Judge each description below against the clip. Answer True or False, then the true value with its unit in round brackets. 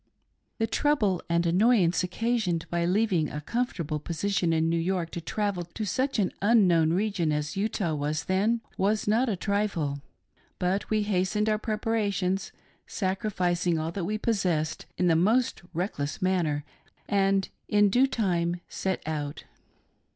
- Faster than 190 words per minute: False (150 wpm)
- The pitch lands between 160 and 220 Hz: True (190 Hz)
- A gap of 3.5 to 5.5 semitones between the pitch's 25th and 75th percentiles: True (4.0 semitones)